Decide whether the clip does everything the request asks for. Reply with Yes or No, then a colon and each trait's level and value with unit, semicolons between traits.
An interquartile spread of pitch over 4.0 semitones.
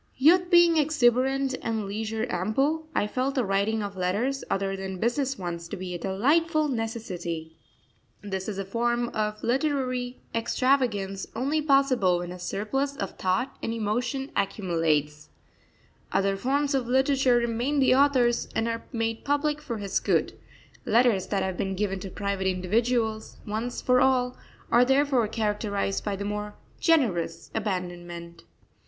Yes: average, 5.3 semitones